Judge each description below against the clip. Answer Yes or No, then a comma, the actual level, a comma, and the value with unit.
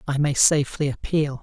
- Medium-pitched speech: Yes, medium, 145 Hz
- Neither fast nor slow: Yes, average, 170 wpm